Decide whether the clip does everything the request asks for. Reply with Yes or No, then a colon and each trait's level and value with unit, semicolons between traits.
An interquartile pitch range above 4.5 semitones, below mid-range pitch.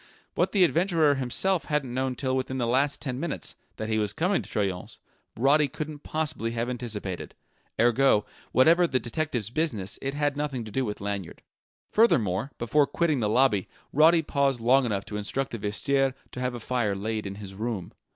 Yes: average, 5.2 semitones; low, 125 Hz